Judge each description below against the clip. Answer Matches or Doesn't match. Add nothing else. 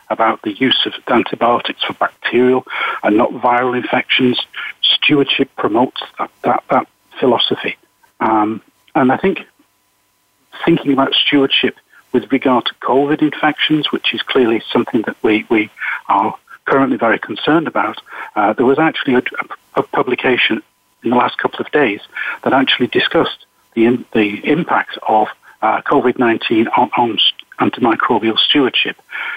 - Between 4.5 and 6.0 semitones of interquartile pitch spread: Doesn't match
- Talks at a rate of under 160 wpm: Matches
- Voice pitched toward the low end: Matches